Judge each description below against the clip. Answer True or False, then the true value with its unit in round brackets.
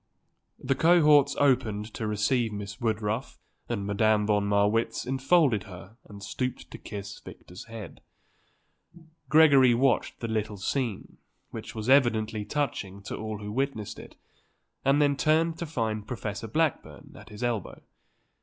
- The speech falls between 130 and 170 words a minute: True (140 wpm)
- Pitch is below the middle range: True (110 Hz)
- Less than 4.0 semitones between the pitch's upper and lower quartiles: False (4.6 semitones)